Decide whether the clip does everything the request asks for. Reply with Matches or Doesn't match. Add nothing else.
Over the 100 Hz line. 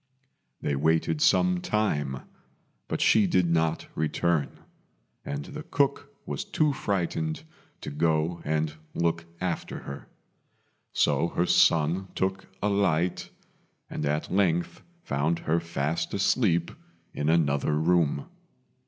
Doesn't match